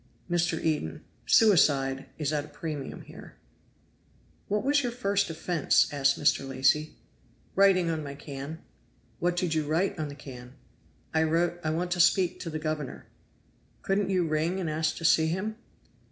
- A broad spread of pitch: No, average, 3.4 semitones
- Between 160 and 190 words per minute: Yes, average, 165 wpm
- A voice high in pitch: No, medium, 160 Hz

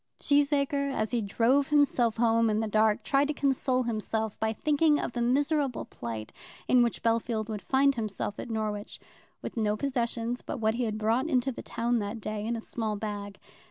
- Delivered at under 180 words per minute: No, average, 195 wpm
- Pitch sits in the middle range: No, high, 230 Hz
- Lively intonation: No, average, 3.8 semitones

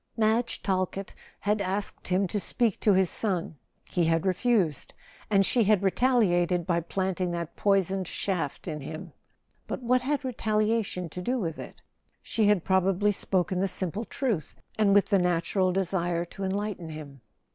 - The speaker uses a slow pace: No, average, 160 wpm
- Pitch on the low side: No, high, 190 Hz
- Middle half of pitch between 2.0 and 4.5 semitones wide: Yes, average, 3.1 semitones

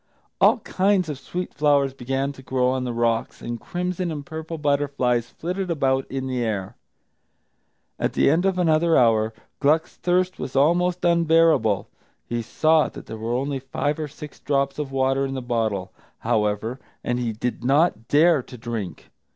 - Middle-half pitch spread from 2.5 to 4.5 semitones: No, average, 4.9 semitones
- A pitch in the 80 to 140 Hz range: Yes, low, 135 Hz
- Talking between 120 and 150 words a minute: No, average, 170 wpm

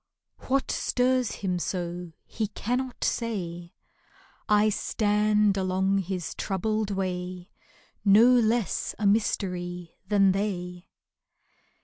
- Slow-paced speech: Yes, slow, 100 wpm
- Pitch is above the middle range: Yes, high, 195 Hz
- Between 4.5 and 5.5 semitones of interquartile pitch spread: No, average, 3.2 semitones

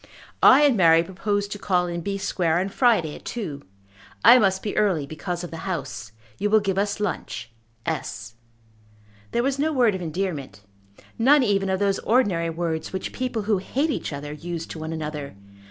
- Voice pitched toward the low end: No, high, 190 Hz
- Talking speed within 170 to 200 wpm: Yes, average, 185 wpm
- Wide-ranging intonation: No, average, 4.4 semitones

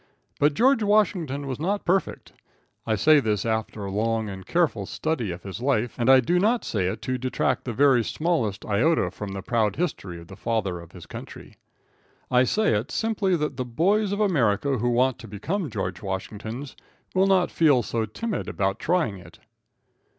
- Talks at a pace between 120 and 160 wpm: No, average, 185 wpm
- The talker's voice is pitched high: No, low, 125 Hz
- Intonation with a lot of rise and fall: Yes, wide, 8.2 semitones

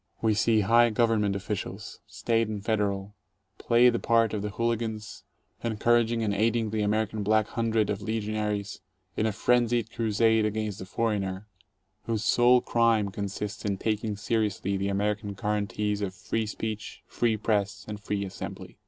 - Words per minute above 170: No, average, 155 wpm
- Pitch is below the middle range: Yes, low, 110 Hz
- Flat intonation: Yes, narrow, 1.8 semitones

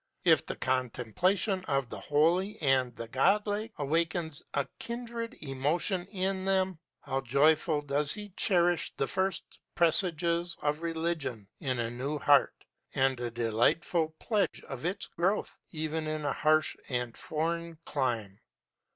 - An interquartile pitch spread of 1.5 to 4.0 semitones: No, average, 5.1 semitones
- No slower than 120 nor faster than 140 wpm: Yes, slow, 135 wpm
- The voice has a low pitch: No, medium, 155 Hz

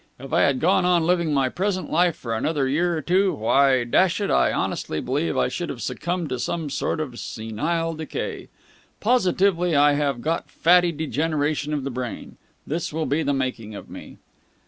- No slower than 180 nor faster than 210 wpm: Yes, average, 190 wpm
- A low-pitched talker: No, medium, 155 Hz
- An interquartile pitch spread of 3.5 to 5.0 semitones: Yes, average, 4.4 semitones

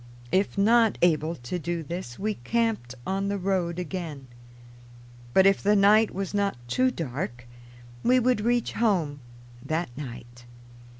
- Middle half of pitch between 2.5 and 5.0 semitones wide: No, wide, 5.5 semitones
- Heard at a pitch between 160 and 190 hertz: Yes, medium, 185 Hz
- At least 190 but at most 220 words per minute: No, average, 140 wpm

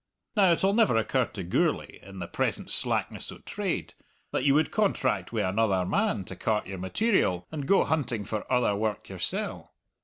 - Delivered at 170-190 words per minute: Yes, average, 180 wpm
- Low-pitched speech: Yes, low, 115 Hz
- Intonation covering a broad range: Yes, wide, 8.5 semitones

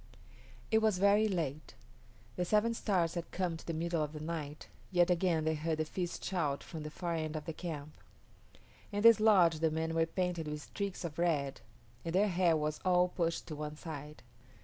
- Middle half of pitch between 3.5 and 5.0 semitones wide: No, average, 2.8 semitones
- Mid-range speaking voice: Yes, medium, 165 Hz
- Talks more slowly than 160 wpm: No, average, 200 wpm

